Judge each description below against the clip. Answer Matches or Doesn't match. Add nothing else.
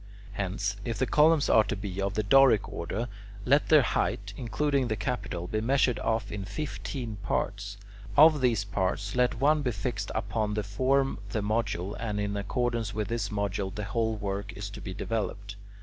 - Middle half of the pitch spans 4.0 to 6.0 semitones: Doesn't match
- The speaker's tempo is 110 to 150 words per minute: Doesn't match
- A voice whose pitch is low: Matches